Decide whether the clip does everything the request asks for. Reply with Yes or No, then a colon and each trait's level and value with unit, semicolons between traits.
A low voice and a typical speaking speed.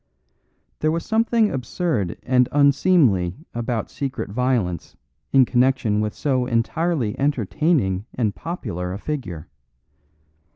No: low, 125 Hz; slow, 110 wpm